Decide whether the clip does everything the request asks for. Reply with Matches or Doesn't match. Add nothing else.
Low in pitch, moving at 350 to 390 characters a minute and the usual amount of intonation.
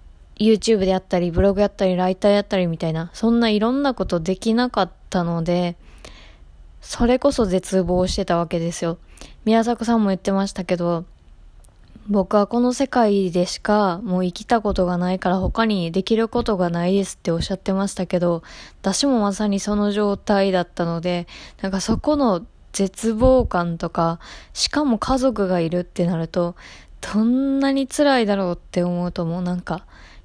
Doesn't match